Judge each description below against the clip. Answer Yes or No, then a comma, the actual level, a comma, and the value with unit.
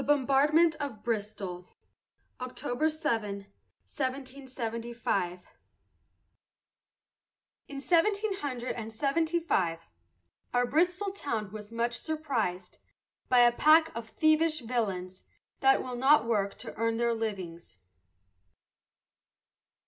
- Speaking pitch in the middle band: No, high, 245 Hz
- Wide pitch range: Yes, wide, 5.8 semitones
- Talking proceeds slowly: Yes, slow, 100 wpm